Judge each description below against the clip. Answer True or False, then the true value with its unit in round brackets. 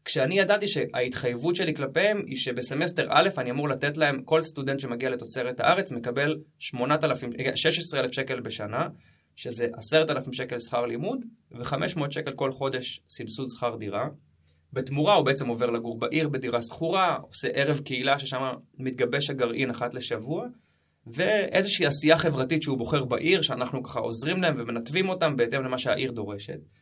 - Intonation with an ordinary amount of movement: True (4.2 semitones)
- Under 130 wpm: False (145 wpm)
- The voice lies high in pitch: False (135 Hz)